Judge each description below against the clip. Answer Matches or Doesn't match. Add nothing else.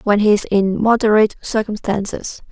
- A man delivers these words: Doesn't match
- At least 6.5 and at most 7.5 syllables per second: Doesn't match